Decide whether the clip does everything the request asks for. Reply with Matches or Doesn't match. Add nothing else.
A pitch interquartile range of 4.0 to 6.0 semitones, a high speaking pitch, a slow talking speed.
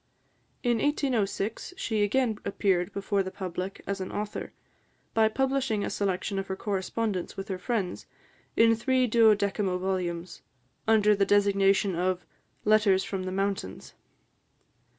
Doesn't match